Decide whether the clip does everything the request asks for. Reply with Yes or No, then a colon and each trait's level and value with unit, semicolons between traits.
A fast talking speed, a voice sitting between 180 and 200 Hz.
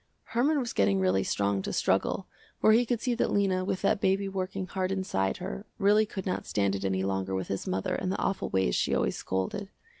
Yes: fast, 220 wpm; medium, 185 Hz